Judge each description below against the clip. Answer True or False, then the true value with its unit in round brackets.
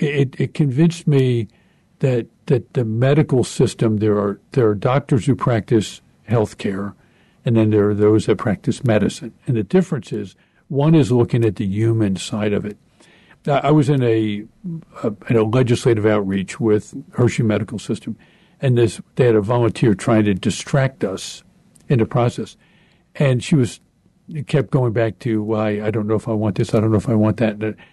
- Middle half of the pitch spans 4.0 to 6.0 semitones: True (4.4 semitones)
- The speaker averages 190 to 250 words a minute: True (200 wpm)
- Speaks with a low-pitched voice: True (120 Hz)